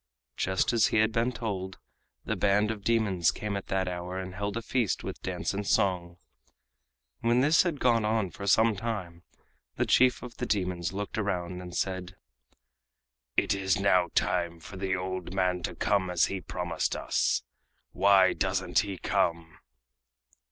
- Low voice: Yes, very low, 95 Hz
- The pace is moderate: Yes, average, 165 wpm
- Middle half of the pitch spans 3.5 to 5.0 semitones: No, average, 2.9 semitones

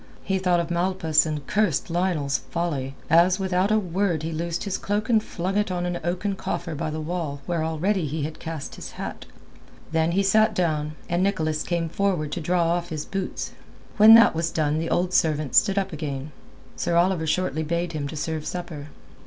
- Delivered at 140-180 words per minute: No, average, 200 wpm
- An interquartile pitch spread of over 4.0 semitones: No, average, 3.0 semitones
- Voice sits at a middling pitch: Yes, medium, 170 Hz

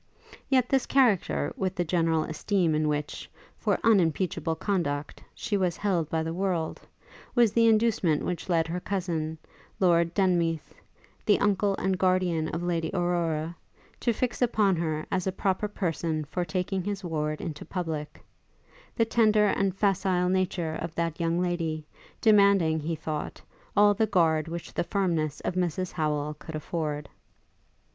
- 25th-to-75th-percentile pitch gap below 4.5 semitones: Yes, average, 3.5 semitones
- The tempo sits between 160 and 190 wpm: No, average, 150 wpm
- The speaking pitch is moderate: Yes, medium, 175 Hz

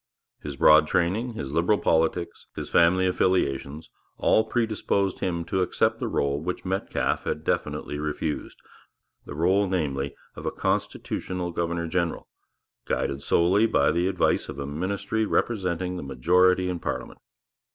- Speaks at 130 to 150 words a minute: Yes, average, 140 wpm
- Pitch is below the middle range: Yes, very low, 85 Hz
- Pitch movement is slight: No, average, 3.4 semitones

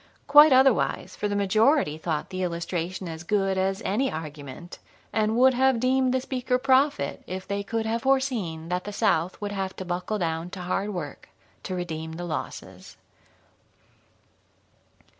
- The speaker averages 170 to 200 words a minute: No, average, 160 wpm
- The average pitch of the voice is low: No, high, 195 Hz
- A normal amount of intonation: No, wide, 6.2 semitones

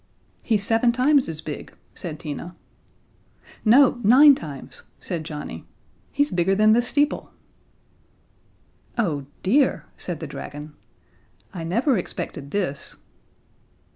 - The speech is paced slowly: Yes, slow, 110 wpm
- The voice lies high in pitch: Yes, high, 200 Hz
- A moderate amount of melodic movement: No, wide, 7.7 semitones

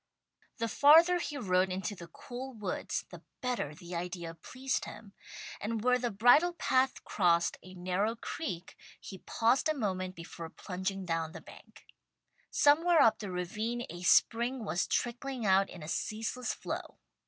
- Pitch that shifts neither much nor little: No, wide, 5.7 semitones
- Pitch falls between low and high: No, high, 215 Hz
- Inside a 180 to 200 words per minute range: No, average, 155 wpm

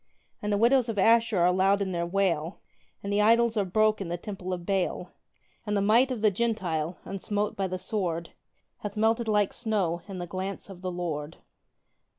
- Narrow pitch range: No, average, 3.2 semitones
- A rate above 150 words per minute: Yes, average, 195 wpm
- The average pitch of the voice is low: No, high, 195 Hz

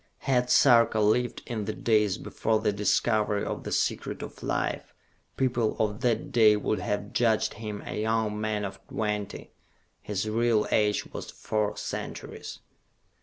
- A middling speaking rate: Yes, average, 150 wpm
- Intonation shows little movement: Yes, narrow, 1.6 semitones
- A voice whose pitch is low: Yes, low, 110 Hz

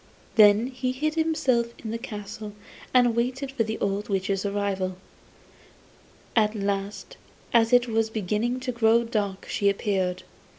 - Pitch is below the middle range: No, high, 220 Hz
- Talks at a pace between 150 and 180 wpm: No, slow, 135 wpm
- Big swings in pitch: No, average, 3.2 semitones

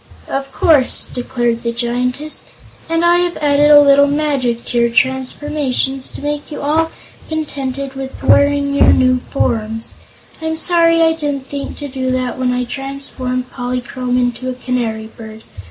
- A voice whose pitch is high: Yes, very high, 265 Hz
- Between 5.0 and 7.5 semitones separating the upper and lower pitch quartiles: No, average, 2.8 semitones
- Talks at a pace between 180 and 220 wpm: No, average, 155 wpm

